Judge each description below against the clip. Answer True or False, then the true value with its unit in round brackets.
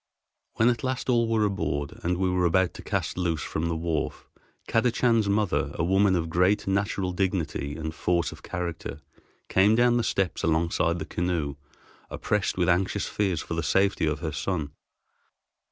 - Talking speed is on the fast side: False (170 wpm)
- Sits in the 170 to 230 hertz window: False (90 Hz)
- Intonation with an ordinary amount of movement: True (3.6 semitones)